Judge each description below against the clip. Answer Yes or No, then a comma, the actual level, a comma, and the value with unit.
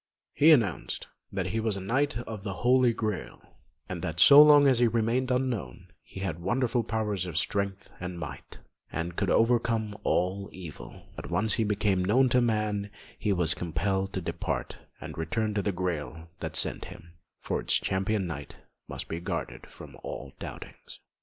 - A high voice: No, low, 100 Hz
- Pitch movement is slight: No, average, 4.3 semitones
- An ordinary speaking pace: Yes, average, 175 wpm